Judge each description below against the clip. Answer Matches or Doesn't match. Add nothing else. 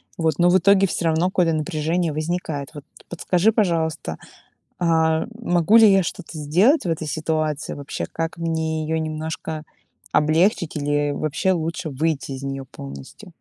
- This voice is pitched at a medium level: Matches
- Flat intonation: Matches